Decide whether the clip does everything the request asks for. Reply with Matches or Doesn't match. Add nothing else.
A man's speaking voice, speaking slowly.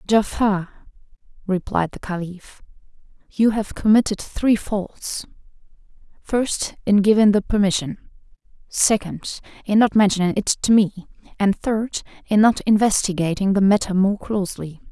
Doesn't match